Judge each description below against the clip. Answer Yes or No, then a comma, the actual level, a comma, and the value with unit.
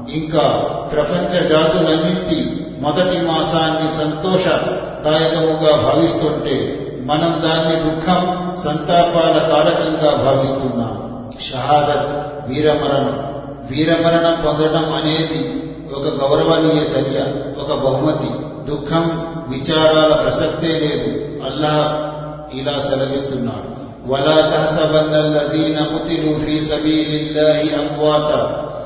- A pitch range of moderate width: No, narrow, 1.6 semitones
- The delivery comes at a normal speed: No, slow, 65 wpm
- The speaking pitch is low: No, medium, 155 Hz